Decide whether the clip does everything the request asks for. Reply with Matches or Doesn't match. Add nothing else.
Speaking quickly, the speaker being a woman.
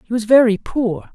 Matches